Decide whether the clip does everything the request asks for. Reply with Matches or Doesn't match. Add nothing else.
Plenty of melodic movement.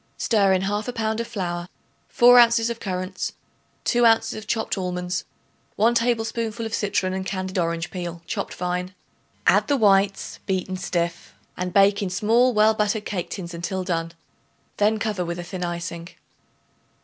Doesn't match